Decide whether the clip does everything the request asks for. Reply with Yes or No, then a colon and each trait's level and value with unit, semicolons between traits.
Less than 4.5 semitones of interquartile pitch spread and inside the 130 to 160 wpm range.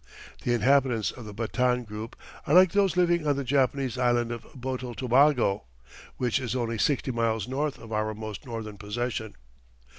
No: average, 3.3 semitones; average, 170 wpm